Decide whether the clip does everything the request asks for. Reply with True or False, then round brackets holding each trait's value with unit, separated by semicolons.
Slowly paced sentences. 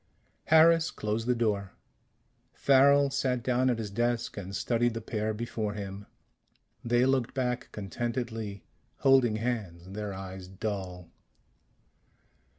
True (120 wpm)